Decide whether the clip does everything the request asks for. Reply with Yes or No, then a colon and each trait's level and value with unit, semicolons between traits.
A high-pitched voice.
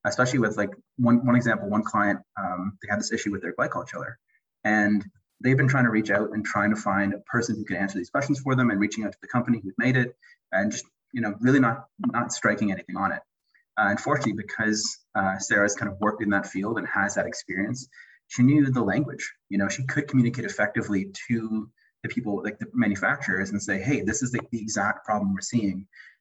No: low, 110 Hz